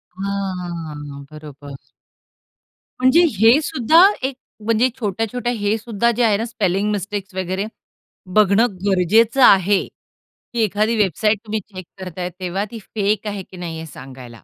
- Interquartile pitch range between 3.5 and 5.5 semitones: Yes, average, 3.8 semitones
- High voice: Yes, high, 200 Hz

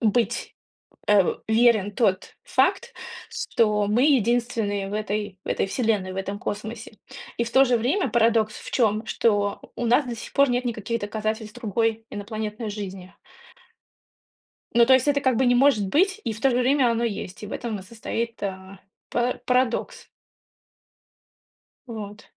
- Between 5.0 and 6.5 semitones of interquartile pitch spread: No, average, 2.8 semitones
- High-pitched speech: Yes, high, 225 Hz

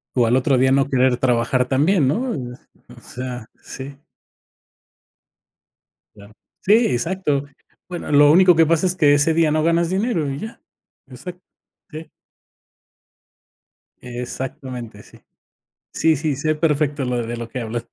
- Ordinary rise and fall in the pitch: Yes, average, 4.6 semitones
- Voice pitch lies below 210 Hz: Yes, medium, 140 Hz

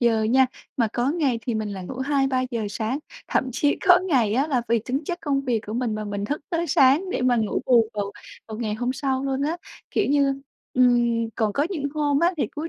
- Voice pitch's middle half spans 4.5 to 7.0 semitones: No, average, 4.0 semitones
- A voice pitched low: No, very high, 255 Hz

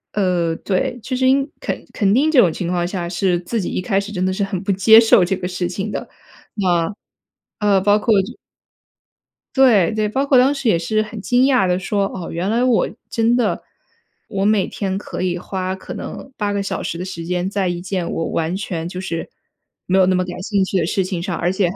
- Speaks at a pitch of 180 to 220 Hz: Yes, high, 190 Hz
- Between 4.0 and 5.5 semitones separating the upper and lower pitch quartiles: No, average, 3.1 semitones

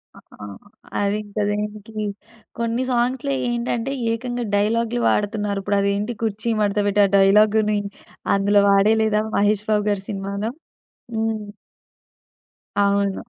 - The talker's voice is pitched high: Yes, high, 210 Hz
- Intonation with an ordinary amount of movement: No, narrow, 2.0 semitones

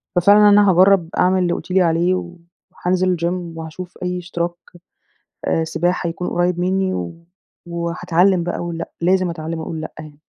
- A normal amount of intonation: No, narrow, 1.6 semitones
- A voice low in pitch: No, medium, 175 Hz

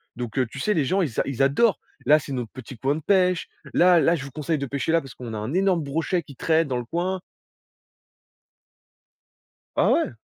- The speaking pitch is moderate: Yes, medium, 145 Hz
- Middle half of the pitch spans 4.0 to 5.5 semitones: Yes, average, 4.9 semitones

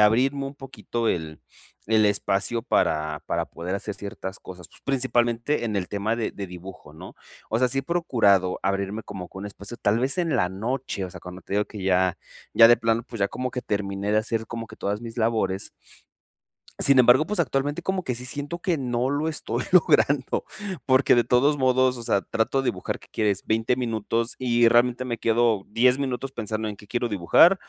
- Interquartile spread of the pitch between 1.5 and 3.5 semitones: No, average, 4.3 semitones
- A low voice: Yes, low, 115 Hz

